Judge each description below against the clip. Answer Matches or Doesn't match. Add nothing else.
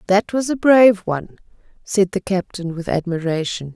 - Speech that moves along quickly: Doesn't match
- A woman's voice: Matches